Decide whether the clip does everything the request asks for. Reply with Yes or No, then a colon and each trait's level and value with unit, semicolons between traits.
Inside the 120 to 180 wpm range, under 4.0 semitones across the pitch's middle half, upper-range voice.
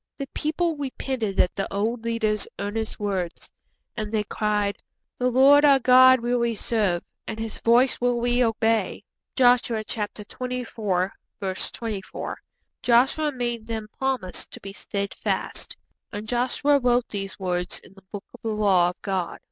Yes: average, 150 wpm; average, 3.5 semitones; high, 225 Hz